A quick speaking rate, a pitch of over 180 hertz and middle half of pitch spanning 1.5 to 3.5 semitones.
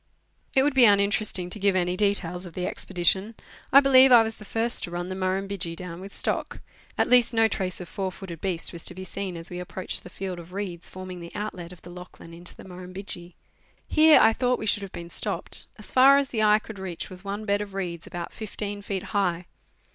Yes: fast, 230 wpm; high, 190 Hz; average, 3.1 semitones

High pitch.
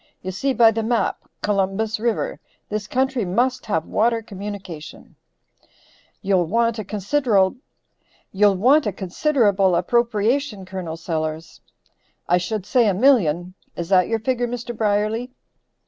Yes: high, 210 Hz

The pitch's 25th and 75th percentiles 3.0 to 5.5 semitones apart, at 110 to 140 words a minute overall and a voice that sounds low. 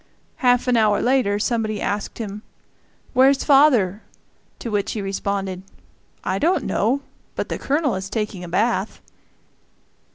No: average, 4.4 semitones; slow, 135 wpm; high, 215 Hz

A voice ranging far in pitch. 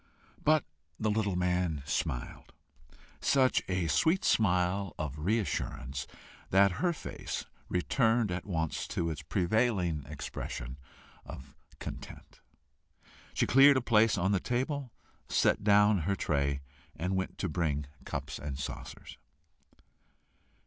Yes: wide, 6.2 semitones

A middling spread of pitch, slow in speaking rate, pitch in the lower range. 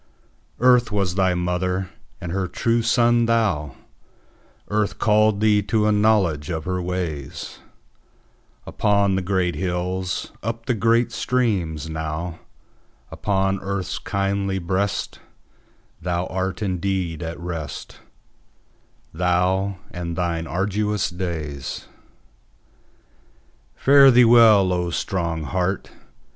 Yes: average, 3.2 semitones; slow, 95 wpm; very low, 95 Hz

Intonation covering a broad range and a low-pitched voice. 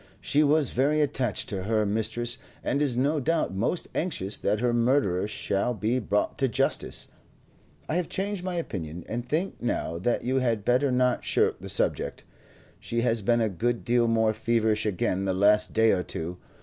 No: average, 4.2 semitones; low, 120 Hz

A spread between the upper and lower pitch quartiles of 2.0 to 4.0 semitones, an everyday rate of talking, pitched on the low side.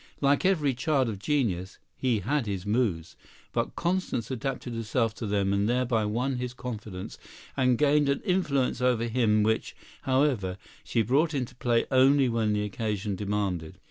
No: average, 4.4 semitones; average, 160 wpm; low, 120 Hz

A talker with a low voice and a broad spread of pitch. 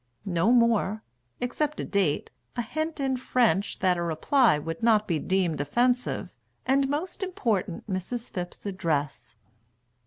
No: high, 210 Hz; wide, 6.3 semitones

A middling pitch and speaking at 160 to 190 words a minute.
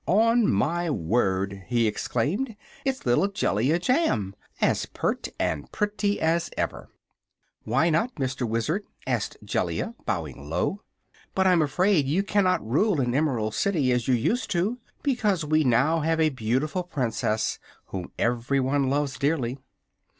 No: medium, 145 Hz; average, 140 wpm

